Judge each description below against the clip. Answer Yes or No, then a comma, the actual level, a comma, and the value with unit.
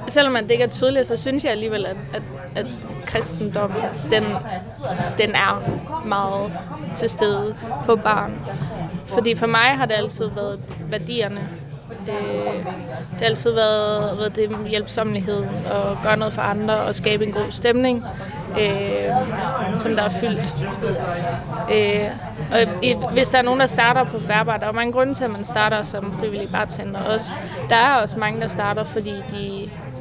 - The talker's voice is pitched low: No, high, 210 Hz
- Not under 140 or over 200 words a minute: Yes, average, 160 wpm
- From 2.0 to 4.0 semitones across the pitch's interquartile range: Yes, average, 3.3 semitones